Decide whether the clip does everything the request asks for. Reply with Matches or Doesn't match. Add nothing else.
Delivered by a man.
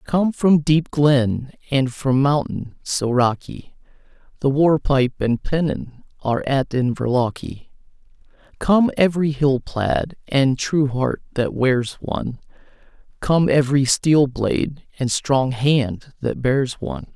Matches